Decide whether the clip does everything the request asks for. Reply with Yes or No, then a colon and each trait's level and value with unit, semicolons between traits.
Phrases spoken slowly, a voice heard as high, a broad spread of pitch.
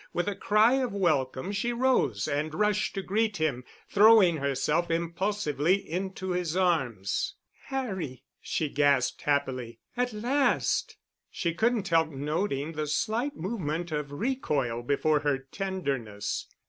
No: slow, 130 wpm; medium, 170 Hz; wide, 6.5 semitones